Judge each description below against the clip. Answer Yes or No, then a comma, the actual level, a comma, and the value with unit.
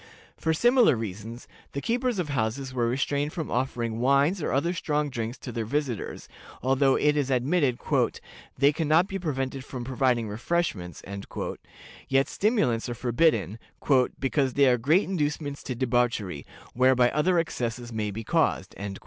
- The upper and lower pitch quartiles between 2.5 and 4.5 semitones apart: Yes, average, 4.1 semitones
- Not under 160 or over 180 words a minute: No, average, 150 wpm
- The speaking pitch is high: No, low, 135 Hz